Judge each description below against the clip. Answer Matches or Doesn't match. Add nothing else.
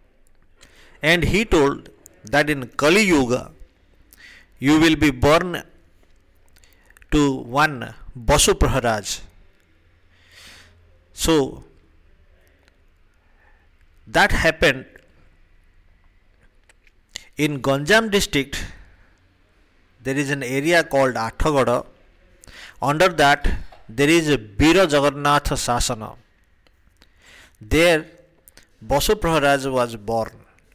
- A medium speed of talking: Doesn't match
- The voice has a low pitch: Matches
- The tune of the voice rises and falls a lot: Matches